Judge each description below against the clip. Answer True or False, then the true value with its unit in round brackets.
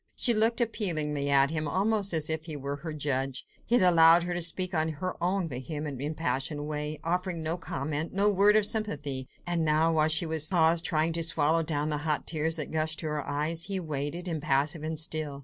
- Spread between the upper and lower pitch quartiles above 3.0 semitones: False (2.7 semitones)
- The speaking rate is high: True (210 wpm)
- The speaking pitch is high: False (160 Hz)